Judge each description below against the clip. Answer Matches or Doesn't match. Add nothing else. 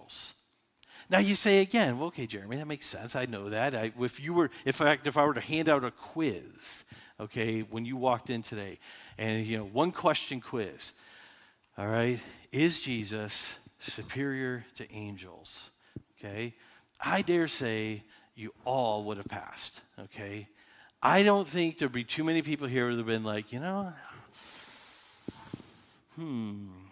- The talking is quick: Doesn't match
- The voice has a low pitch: Matches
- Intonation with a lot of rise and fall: Matches